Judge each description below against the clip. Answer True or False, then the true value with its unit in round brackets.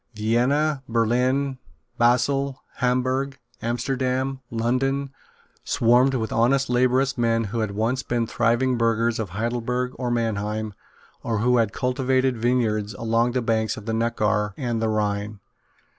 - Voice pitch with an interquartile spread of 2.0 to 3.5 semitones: True (2.4 semitones)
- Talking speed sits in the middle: False (130 wpm)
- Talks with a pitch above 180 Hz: False (120 Hz)